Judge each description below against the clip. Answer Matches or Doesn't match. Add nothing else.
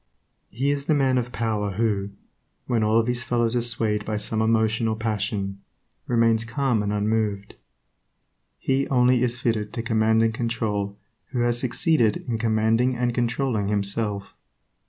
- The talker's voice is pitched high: Doesn't match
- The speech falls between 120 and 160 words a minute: Matches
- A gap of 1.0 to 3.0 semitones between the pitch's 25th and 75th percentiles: Matches